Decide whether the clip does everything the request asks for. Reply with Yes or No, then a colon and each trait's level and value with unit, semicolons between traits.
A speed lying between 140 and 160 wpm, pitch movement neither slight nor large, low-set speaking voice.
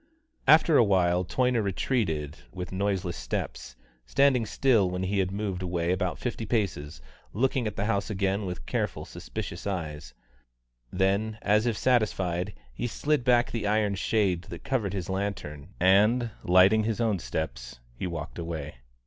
Yes: average, 155 wpm; average, 3.9 semitones; very low, 95 Hz